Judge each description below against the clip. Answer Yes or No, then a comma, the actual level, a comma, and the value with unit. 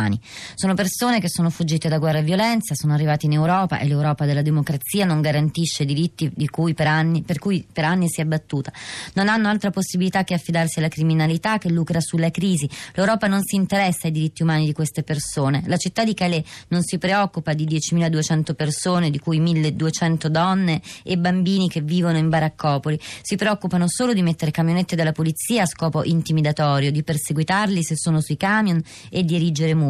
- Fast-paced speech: Yes, fast, 190 wpm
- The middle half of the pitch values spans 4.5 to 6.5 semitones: No, average, 2.8 semitones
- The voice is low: No, medium, 165 Hz